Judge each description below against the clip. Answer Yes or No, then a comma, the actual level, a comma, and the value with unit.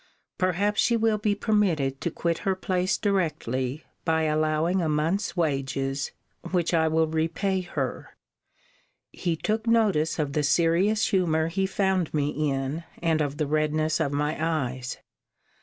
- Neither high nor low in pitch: Yes, medium, 160 Hz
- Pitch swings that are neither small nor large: Yes, average, 4.0 semitones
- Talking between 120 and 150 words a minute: Yes, average, 145 wpm